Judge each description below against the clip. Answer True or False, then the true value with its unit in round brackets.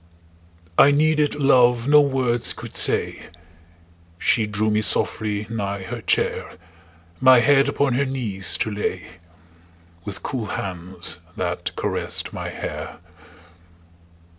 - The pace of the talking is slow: True (115 wpm)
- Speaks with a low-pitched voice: True (120 Hz)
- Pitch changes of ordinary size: True (4.9 semitones)